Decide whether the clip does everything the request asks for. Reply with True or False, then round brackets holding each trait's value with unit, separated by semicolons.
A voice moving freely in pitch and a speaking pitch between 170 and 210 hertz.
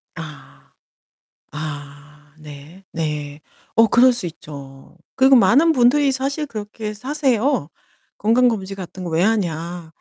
True (8.2 semitones; 190 Hz)